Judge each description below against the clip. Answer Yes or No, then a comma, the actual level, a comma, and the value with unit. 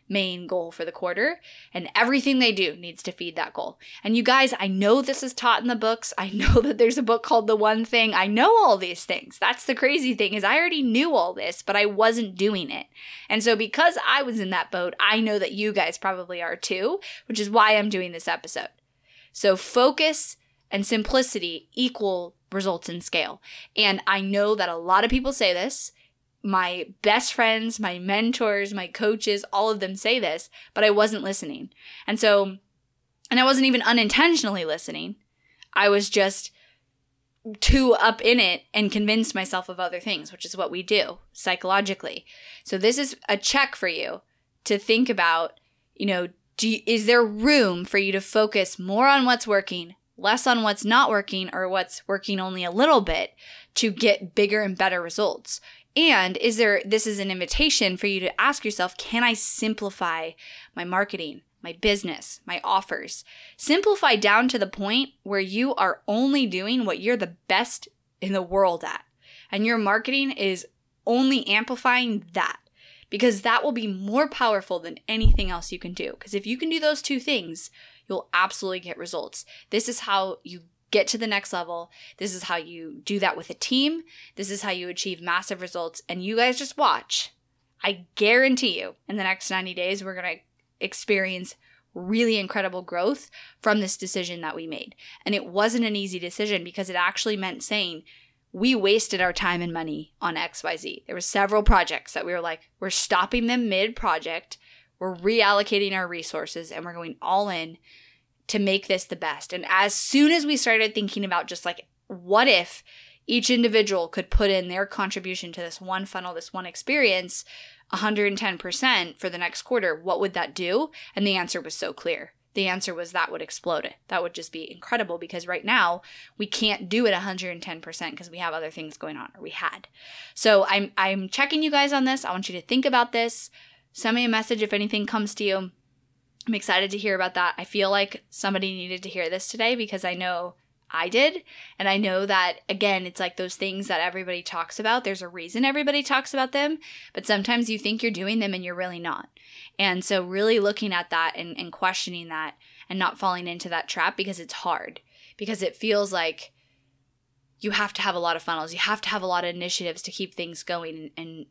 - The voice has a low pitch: No, high, 200 Hz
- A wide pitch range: No, average, 4.0 semitones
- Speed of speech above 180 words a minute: Yes, average, 200 wpm